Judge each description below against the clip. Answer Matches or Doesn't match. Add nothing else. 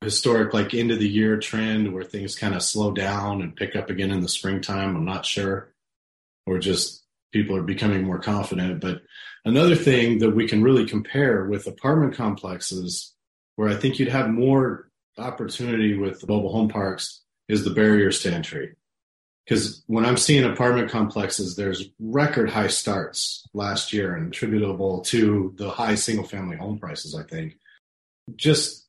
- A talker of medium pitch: Doesn't match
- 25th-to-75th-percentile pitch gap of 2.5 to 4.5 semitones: Matches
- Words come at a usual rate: Matches